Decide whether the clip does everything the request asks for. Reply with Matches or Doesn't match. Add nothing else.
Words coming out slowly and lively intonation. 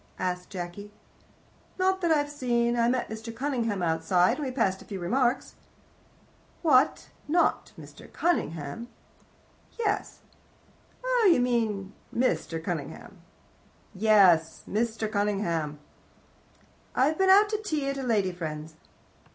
Matches